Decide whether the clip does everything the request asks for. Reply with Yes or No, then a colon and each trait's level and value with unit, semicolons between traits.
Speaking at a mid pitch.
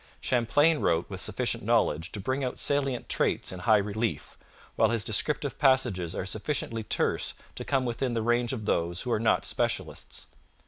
No: low, 115 Hz